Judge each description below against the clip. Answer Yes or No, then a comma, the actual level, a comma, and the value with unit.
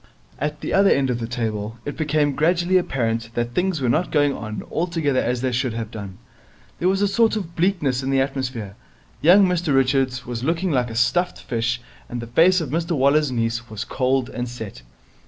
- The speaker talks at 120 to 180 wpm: No, fast, 205 wpm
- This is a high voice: No, low, 135 Hz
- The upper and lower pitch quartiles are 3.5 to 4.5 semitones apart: No, wide, 5.6 semitones